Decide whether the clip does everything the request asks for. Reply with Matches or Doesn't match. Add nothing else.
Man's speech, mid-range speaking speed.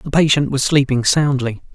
Matches